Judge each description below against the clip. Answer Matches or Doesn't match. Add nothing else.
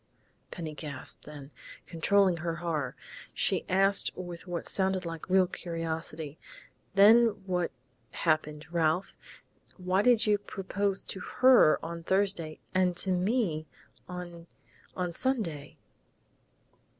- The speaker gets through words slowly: Matches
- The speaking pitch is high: Doesn't match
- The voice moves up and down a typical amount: Matches